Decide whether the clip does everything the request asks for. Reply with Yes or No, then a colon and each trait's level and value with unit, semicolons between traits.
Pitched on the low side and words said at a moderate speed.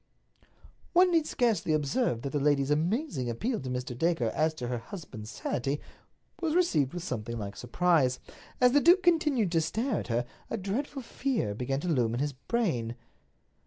No: medium, 155 Hz; average, 175 wpm